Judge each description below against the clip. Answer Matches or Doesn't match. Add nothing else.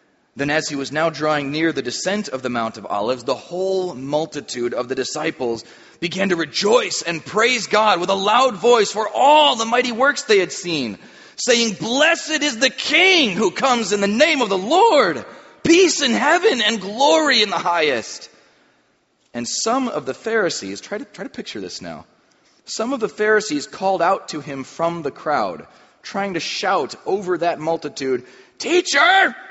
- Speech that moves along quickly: Doesn't match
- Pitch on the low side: Doesn't match